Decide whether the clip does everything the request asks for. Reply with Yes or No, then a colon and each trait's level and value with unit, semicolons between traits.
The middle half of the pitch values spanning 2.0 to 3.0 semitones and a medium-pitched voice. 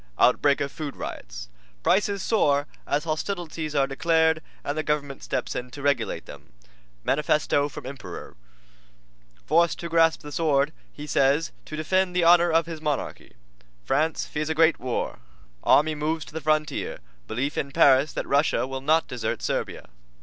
Yes: narrow, 2.6 semitones; medium, 150 Hz